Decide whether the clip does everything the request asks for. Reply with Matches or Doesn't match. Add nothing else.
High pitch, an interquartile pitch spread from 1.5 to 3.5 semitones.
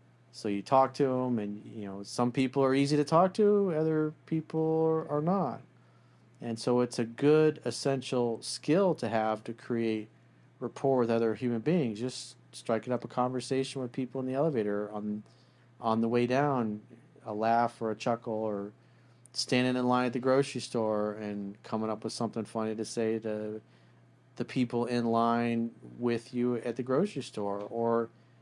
Doesn't match